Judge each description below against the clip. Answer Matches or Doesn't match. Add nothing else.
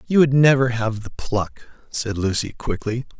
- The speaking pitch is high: Doesn't match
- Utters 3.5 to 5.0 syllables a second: Matches